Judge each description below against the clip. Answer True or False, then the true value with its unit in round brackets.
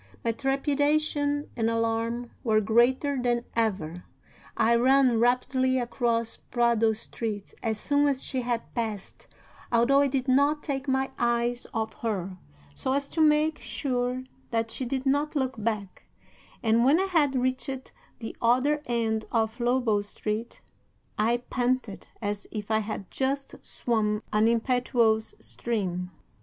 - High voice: True (240 Hz)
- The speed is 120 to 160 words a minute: True (140 wpm)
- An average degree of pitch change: True (3.1 semitones)